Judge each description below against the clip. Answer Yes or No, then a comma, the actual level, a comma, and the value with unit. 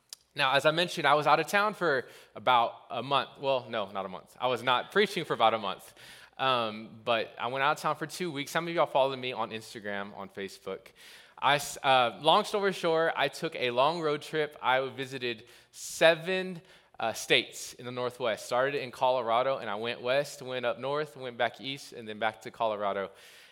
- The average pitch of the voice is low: Yes, low, 130 Hz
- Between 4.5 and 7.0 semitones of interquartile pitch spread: Yes, wide, 5.4 semitones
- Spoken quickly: Yes, fast, 210 wpm